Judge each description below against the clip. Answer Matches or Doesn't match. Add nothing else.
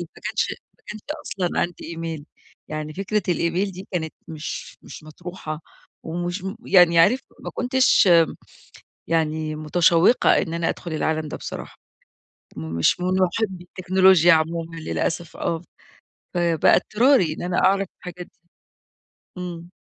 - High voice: Doesn't match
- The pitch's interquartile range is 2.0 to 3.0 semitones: Matches